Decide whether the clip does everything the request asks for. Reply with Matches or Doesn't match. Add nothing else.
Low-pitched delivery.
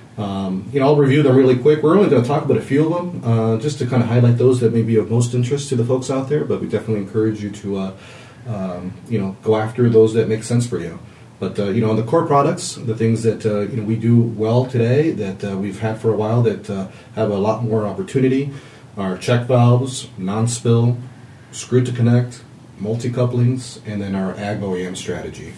Matches